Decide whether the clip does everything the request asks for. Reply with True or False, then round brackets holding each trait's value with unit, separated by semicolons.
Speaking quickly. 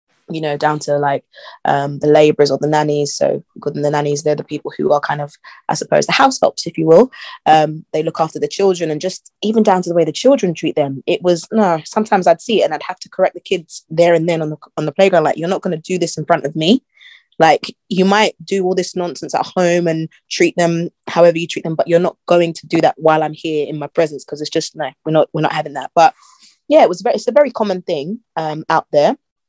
True (270 wpm)